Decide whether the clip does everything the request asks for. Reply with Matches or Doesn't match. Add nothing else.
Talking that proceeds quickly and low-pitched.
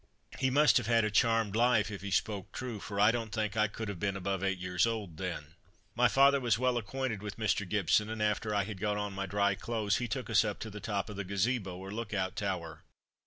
Matches